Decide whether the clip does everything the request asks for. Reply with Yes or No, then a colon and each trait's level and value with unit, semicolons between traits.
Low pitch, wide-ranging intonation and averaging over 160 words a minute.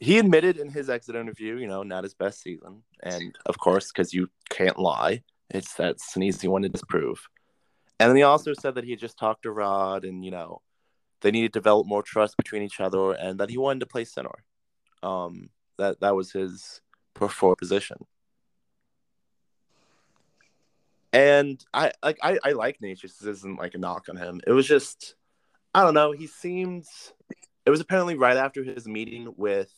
Yes: low, 110 Hz; wide, 6.2 semitones; average, 185 wpm